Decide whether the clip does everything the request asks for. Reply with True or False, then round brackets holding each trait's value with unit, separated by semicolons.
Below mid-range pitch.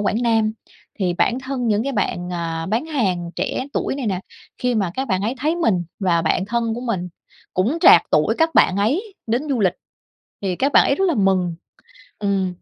False (215 Hz)